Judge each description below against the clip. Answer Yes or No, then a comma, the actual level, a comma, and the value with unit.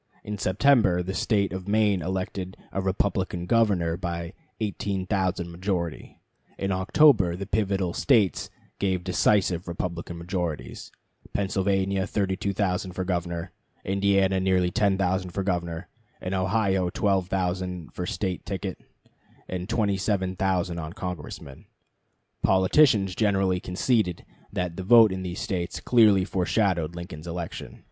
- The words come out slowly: Yes, slow, 115 wpm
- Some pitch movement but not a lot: No, narrow, 1.9 semitones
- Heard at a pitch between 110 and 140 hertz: No, very low, 95 Hz